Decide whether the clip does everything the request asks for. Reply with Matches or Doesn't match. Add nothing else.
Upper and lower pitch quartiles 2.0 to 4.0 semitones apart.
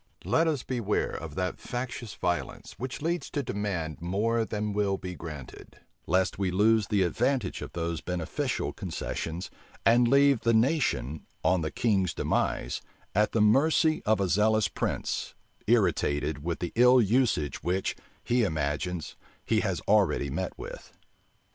Doesn't match